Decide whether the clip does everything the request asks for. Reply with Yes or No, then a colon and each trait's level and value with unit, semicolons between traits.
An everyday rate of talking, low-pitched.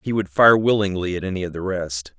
No: fast, 245 wpm; very low, 95 Hz